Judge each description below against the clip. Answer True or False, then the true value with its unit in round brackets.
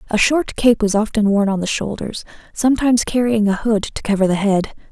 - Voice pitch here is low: False (215 Hz)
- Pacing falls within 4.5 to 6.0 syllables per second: True (5.6 syllables/s)